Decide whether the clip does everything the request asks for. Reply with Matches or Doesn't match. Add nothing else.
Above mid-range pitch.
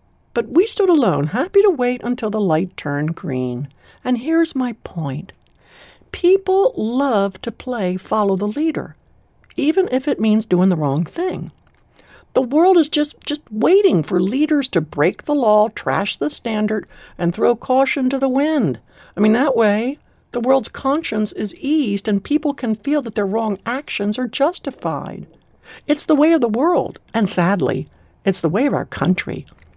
Matches